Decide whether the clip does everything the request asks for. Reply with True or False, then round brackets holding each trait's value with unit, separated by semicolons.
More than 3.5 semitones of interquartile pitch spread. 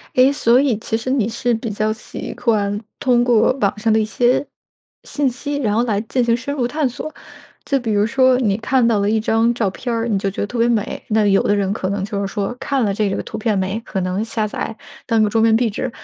False (2.9 semitones)